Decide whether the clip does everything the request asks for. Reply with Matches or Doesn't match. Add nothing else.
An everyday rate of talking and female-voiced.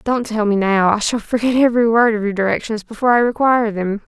Doesn't match